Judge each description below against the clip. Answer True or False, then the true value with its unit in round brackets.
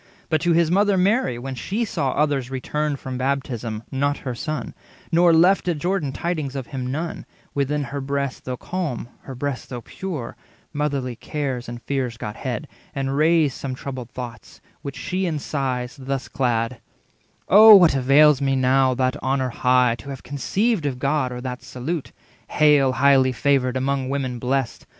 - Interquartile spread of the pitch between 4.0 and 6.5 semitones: False (3.0 semitones)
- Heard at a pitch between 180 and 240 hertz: False (135 Hz)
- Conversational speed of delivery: True (175 wpm)